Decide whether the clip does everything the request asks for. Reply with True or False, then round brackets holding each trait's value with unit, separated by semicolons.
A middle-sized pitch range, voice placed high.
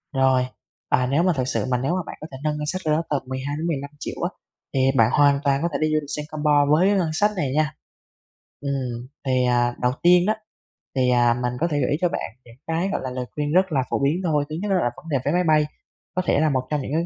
False (3.6 semitones; 145 Hz)